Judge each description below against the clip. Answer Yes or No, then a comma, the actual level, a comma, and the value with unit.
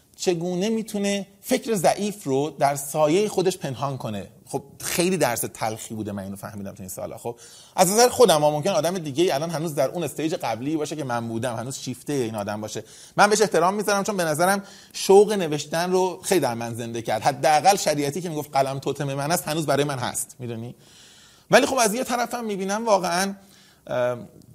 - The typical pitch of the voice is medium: Yes, medium, 155 Hz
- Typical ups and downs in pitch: No, wide, 7.2 semitones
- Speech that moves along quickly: Yes, fast, 195 wpm